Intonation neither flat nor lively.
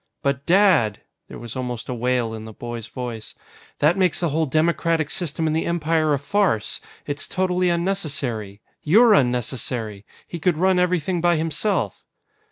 No: wide, 6.3 semitones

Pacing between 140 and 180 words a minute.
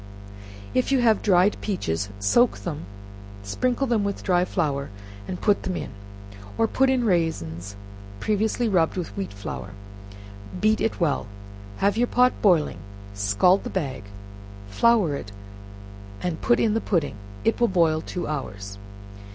Yes: average, 150 wpm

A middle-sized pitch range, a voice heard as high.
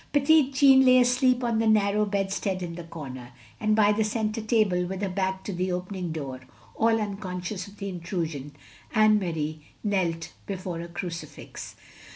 Yes: average, 3.7 semitones; high, 195 Hz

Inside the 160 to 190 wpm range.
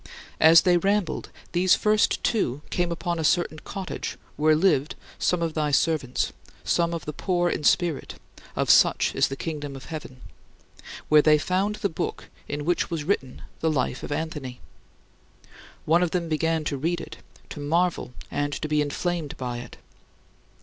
Yes: average, 170 wpm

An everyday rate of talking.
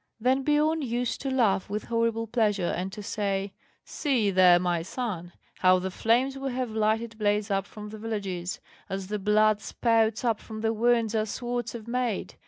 Yes: average, 185 wpm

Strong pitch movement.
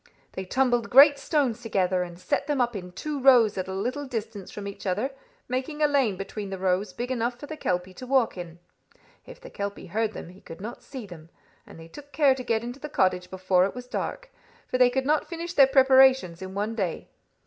Yes: wide, 6.0 semitones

